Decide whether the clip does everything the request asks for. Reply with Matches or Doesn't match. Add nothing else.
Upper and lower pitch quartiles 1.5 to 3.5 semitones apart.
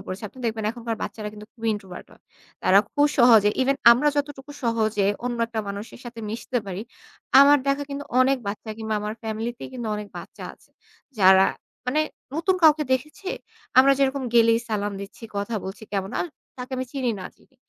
Doesn't match